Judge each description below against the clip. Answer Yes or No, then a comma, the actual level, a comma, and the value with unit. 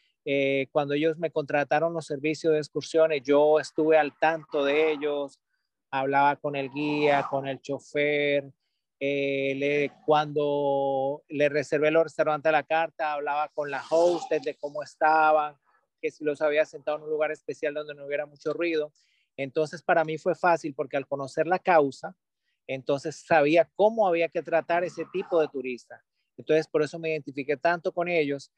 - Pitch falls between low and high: Yes, medium, 150 Hz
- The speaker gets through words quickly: No, average, 170 wpm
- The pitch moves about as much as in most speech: No, narrow, 1.9 semitones